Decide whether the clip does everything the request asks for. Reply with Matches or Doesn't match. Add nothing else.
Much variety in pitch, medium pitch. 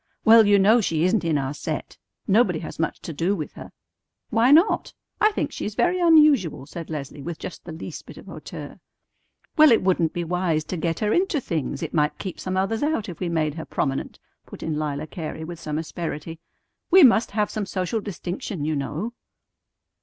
Matches